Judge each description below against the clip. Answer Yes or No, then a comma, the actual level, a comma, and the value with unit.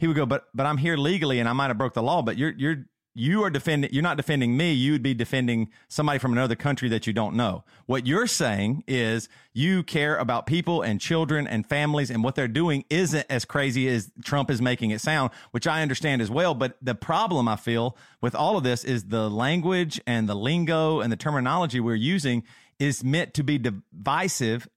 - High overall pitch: No, low, 135 Hz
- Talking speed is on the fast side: Yes, fast, 220 wpm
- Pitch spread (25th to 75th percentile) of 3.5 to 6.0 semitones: Yes, average, 4.5 semitones